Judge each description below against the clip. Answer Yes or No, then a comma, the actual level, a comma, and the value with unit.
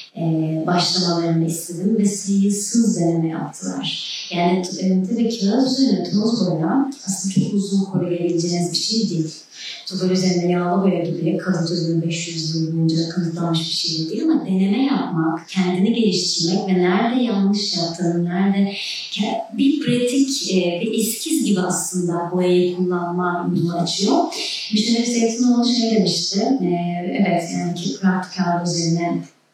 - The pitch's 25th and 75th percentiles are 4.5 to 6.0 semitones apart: No, average, 3.7 semitones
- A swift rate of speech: Yes, fast, 145 wpm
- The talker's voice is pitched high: No, medium, 180 Hz